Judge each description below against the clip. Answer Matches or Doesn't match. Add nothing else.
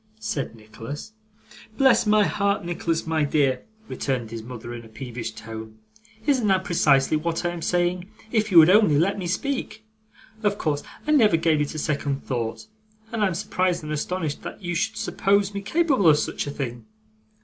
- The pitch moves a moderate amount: Doesn't match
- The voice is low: Doesn't match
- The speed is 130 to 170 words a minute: Doesn't match